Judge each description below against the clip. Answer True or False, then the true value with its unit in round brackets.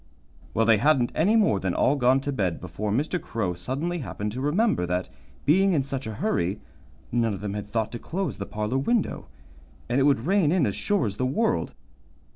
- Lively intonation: True (6.9 semitones)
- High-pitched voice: False (130 Hz)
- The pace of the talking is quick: True (210 wpm)